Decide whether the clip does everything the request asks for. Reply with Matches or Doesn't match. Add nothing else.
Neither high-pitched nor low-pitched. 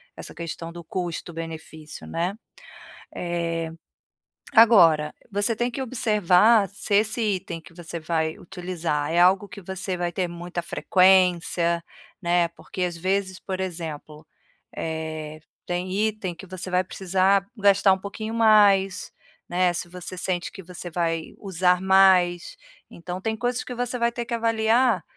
Matches